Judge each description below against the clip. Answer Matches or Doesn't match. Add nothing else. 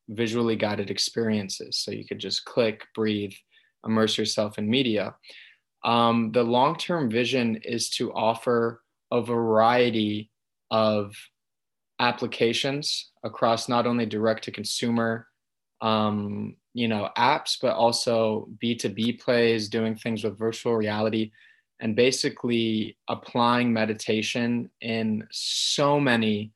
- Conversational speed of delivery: Doesn't match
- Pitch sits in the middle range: Doesn't match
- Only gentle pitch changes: Matches